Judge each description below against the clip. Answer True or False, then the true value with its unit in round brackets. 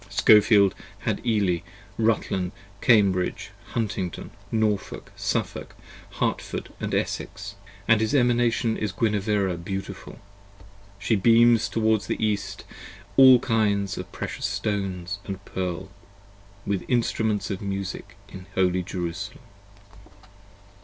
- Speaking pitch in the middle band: False (100 Hz)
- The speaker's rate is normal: False (105 wpm)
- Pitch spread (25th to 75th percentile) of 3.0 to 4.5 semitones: False (2.6 semitones)